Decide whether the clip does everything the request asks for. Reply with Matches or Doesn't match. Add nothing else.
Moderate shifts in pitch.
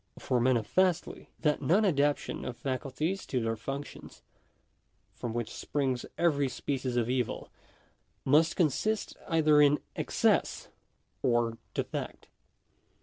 Matches